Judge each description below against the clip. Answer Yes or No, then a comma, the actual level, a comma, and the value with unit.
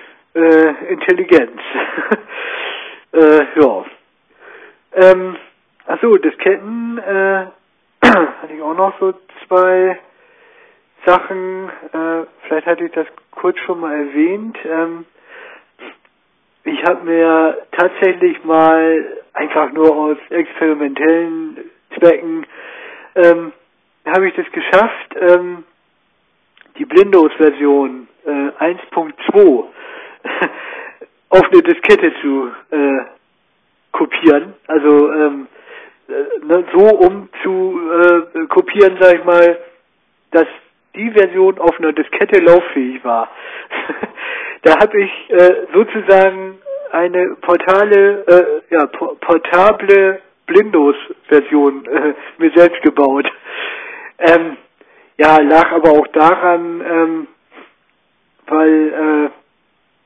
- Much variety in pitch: Yes, wide, 6.6 semitones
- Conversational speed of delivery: No, slow, 95 wpm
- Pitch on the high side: No, medium, 180 Hz